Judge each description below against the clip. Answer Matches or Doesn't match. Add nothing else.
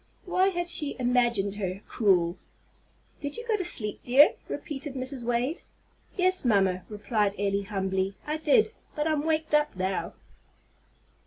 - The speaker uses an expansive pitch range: Matches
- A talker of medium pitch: Doesn't match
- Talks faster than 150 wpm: Doesn't match